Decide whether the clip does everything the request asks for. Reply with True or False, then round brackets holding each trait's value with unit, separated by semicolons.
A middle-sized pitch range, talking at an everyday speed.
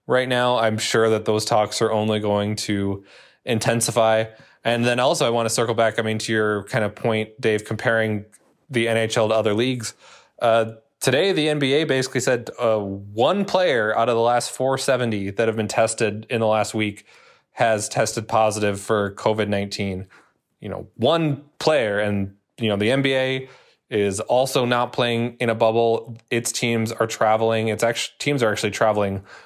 False (2.2 semitones; 180 wpm)